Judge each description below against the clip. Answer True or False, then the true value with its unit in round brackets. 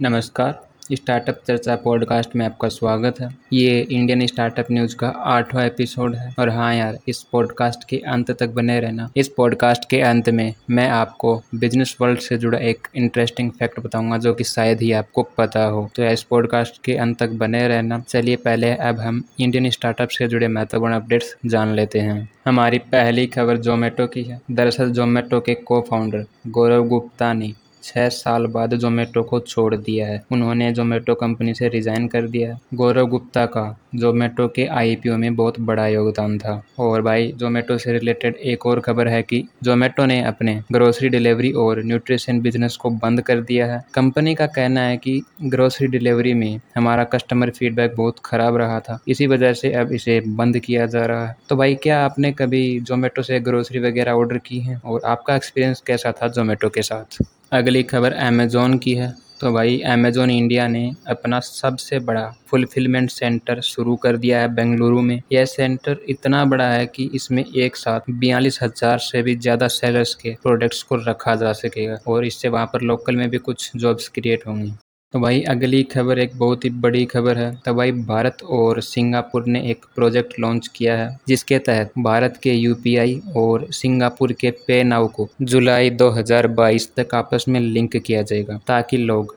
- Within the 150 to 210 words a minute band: True (185 wpm)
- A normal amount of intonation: False (1.2 semitones)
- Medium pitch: False (120 Hz)